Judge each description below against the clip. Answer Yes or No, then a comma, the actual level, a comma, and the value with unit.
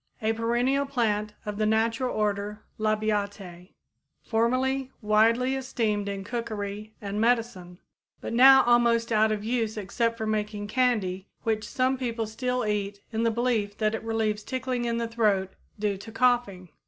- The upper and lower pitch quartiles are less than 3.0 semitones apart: Yes, narrow, 2.5 semitones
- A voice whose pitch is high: Yes, high, 220 Hz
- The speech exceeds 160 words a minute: No, average, 155 wpm